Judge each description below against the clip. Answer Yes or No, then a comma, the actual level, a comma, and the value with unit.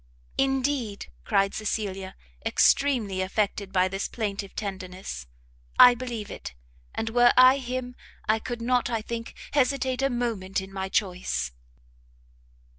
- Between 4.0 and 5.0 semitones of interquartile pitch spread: Yes, average, 4.3 semitones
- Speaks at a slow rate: Yes, slow, 125 wpm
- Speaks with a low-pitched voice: No, high, 220 Hz